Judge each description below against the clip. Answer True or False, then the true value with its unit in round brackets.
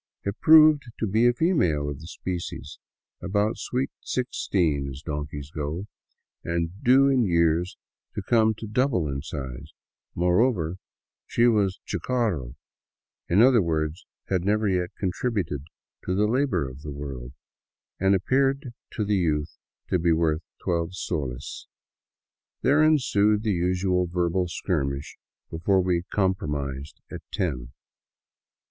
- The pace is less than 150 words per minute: True (135 wpm)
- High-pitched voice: False (90 Hz)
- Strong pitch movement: True (6.1 semitones)